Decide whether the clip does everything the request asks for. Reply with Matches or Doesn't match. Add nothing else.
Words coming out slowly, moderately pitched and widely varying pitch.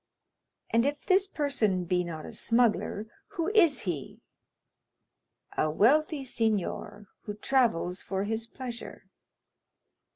Doesn't match